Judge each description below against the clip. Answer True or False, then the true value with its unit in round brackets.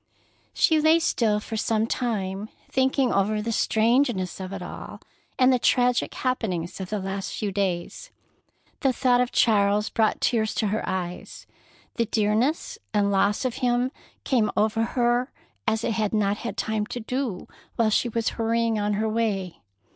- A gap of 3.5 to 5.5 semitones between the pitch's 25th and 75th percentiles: False (3.0 semitones)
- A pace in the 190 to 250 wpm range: False (165 wpm)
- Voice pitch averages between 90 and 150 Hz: False (220 Hz)